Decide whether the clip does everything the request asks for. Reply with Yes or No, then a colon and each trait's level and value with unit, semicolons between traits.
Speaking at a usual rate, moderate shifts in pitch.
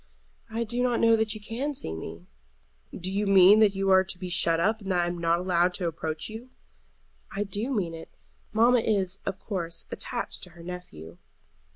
No: fast, 215 wpm; average, 4.1 semitones